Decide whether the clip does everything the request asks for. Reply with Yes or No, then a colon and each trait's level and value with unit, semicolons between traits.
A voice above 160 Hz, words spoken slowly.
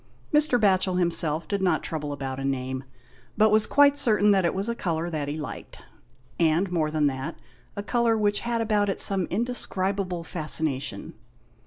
No: medium, 185 Hz; average, 175 wpm